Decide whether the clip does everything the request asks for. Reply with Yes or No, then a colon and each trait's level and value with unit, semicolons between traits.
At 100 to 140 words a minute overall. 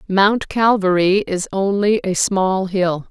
Yes: slow, 135 wpm